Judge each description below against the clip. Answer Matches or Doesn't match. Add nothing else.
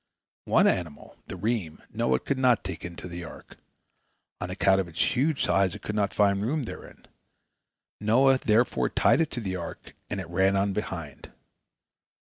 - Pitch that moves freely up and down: Doesn't match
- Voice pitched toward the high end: Doesn't match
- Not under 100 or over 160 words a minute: Doesn't match